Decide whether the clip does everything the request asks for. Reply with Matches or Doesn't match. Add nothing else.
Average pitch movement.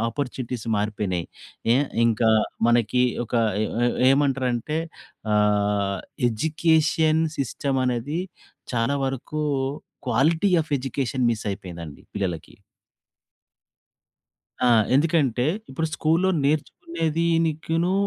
Doesn't match